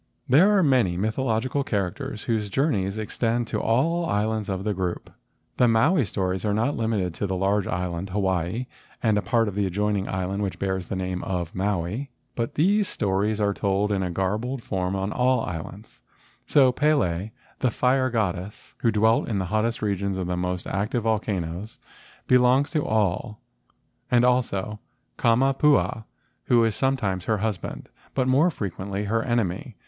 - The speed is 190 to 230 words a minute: No, average, 170 wpm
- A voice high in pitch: No, low, 105 Hz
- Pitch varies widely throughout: No, average, 4.3 semitones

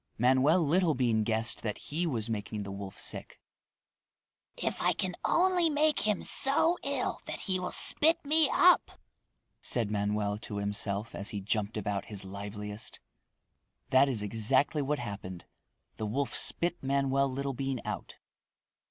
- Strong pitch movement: Yes, wide, 8.5 semitones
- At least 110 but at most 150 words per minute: Yes, average, 145 wpm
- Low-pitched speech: Yes, low, 125 Hz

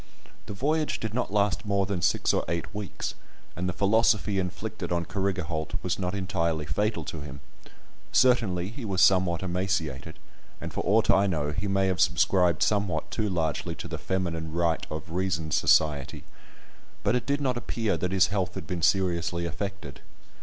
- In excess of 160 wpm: Yes, average, 175 wpm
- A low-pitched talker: Yes, very low, 95 Hz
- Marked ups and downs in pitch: No, average, 3.2 semitones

